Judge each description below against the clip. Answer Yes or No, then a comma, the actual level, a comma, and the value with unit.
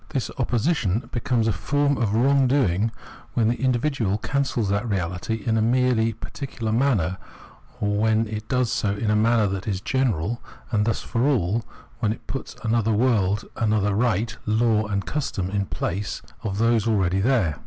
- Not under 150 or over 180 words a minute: Yes, average, 170 wpm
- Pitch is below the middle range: Yes, low, 110 Hz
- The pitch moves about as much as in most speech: Yes, average, 3.1 semitones